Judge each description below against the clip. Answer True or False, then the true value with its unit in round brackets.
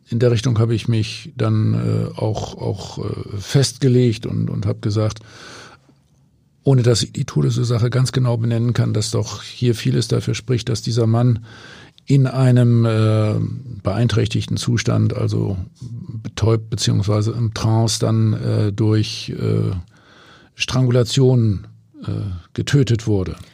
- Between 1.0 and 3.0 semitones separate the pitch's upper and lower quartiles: True (2.4 semitones)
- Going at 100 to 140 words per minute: True (135 wpm)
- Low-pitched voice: True (115 Hz)